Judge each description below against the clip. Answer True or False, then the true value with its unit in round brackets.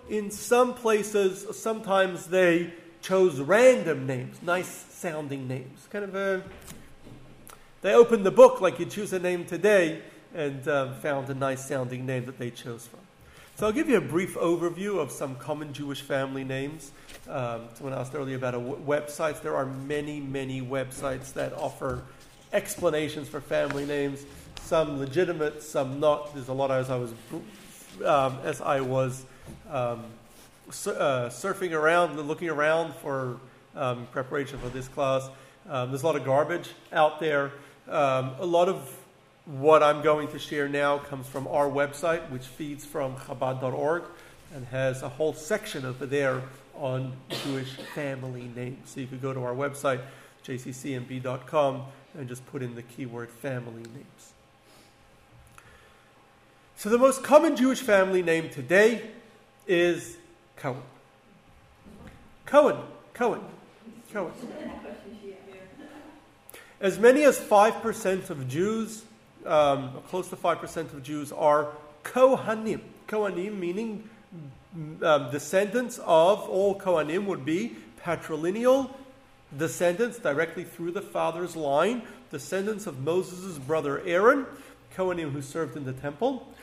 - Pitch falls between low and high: True (150 Hz)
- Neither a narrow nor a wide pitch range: False (5.7 semitones)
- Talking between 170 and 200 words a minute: False (140 wpm)